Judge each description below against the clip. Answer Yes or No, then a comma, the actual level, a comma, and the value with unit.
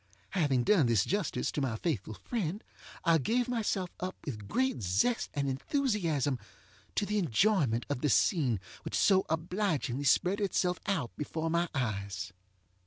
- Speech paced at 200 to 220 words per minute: No, average, 150 wpm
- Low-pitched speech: No, medium, 160 Hz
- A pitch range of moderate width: No, wide, 8.1 semitones